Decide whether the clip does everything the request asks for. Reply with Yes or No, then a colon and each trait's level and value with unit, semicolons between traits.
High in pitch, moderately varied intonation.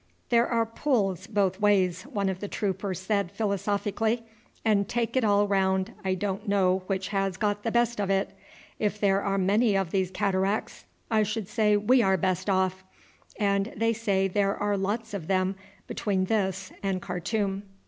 No: high, 200 Hz; narrow, 1.8 semitones